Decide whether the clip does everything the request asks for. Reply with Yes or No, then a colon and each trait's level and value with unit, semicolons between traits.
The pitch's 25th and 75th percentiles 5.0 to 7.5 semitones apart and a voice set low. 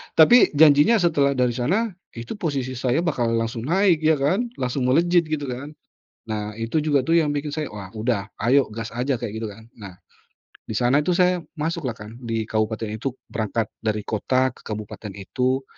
Yes: wide, 5.4 semitones; low, 130 Hz